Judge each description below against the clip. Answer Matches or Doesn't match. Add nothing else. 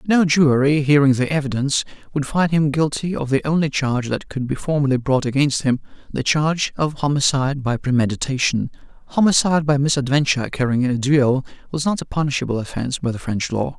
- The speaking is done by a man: Matches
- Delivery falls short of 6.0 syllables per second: Doesn't match